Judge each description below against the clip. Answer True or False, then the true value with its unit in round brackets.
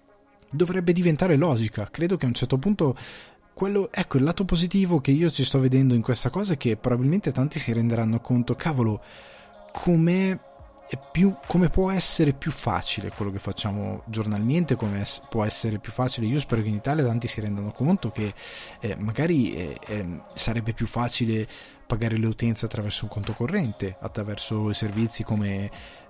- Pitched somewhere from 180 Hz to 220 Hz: False (120 Hz)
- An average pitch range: False (6.3 semitones)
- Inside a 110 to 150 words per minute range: False (165 wpm)